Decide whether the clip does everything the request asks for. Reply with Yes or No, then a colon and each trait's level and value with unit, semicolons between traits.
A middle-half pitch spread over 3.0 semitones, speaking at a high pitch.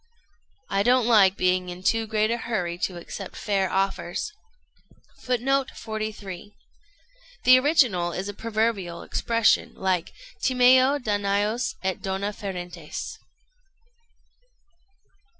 Yes: average, 3.8 semitones; high, 205 Hz